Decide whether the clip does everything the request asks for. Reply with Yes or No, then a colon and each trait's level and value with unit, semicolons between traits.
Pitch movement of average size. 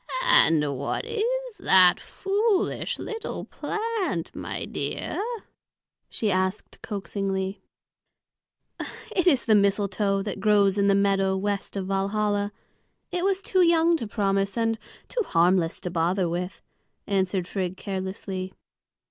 No: wide, 6.7 semitones